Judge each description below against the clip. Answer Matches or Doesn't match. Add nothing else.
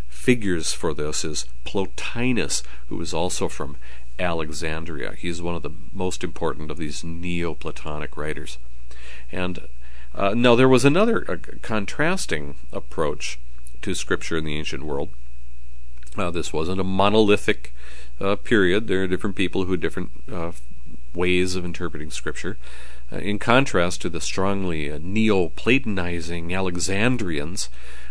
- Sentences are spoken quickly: Doesn't match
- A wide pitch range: Matches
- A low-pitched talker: Matches